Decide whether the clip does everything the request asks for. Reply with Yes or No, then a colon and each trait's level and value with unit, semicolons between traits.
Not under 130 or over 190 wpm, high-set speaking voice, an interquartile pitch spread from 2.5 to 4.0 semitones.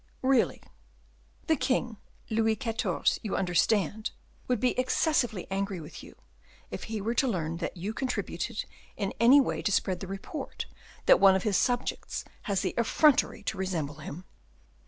No: average, 155 wpm; high, 210 Hz; average, 4.4 semitones